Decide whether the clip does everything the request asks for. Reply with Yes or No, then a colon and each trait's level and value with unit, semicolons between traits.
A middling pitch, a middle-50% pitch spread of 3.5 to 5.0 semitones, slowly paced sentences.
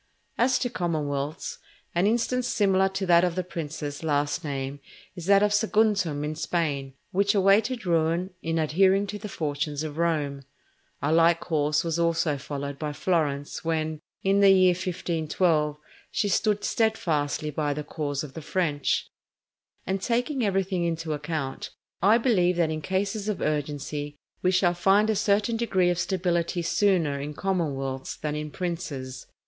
No: medium, 170 Hz; average, 4.5 semitones; average, 155 wpm